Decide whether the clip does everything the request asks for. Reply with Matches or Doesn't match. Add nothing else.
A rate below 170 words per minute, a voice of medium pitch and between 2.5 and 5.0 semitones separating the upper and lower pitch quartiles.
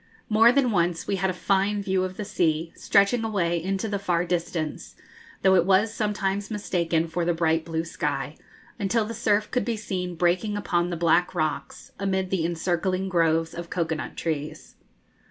Doesn't match